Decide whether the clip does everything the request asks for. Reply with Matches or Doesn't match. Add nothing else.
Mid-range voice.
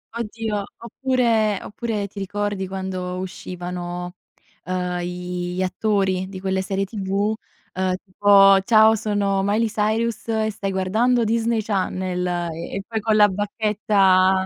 Doesn't match